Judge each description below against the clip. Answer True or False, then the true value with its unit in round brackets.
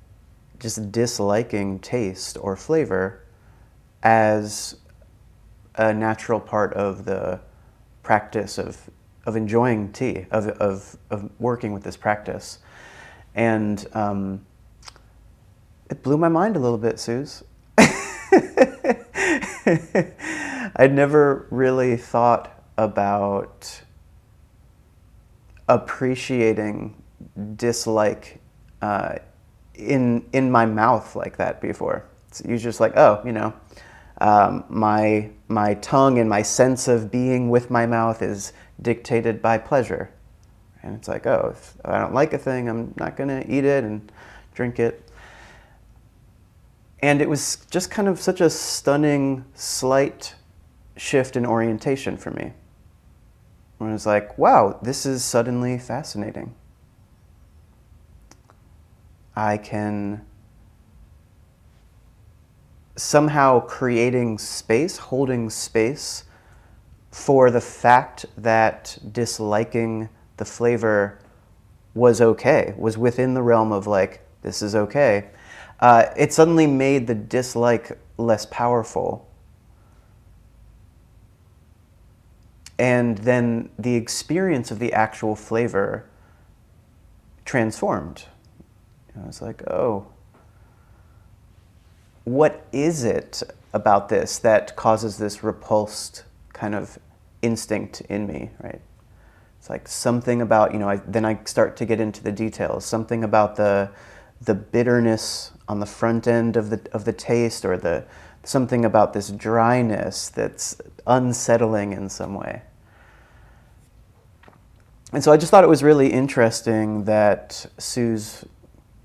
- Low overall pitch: True (110 Hz)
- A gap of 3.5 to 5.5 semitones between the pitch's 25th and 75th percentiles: False (3.0 semitones)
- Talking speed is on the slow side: True (115 wpm)